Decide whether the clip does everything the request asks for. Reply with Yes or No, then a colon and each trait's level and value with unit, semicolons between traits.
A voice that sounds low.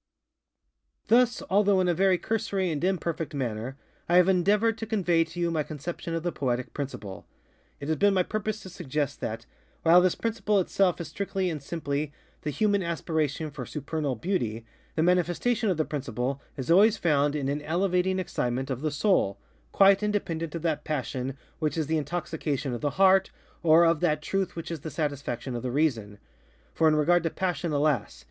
No: medium, 165 Hz